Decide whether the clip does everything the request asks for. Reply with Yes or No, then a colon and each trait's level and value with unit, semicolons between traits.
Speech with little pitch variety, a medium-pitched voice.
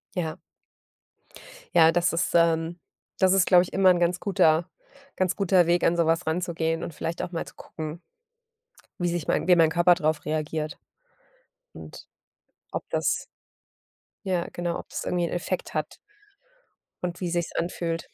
Yes: narrow, 1.5 semitones; medium, 170 Hz